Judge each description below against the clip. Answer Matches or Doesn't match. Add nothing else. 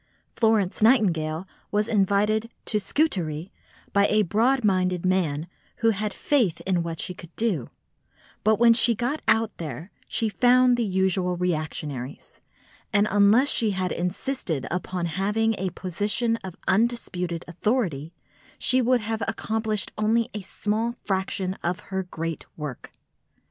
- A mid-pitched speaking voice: Doesn't match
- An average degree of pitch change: Matches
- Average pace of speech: Matches